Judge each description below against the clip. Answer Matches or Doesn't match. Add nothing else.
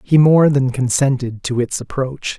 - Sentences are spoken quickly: Doesn't match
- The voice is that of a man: Matches